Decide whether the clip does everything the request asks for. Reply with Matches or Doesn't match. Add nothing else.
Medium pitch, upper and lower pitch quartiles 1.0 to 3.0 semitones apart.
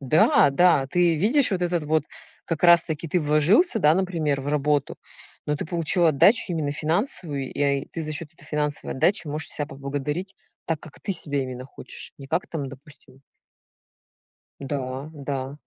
Doesn't match